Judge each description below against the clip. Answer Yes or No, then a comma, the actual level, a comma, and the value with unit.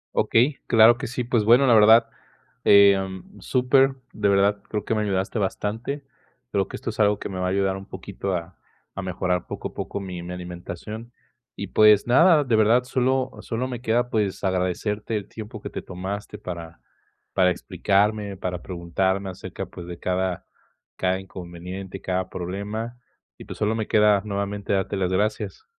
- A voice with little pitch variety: No, average, 3.2 semitones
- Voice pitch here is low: Yes, low, 100 Hz